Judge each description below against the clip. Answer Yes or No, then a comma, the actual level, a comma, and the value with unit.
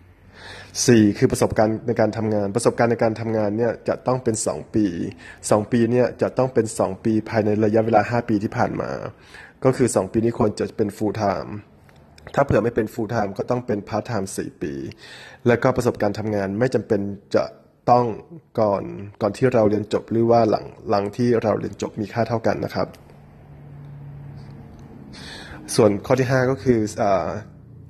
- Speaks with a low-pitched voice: Yes, low, 110 Hz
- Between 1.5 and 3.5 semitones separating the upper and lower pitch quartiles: Yes, average, 2.9 semitones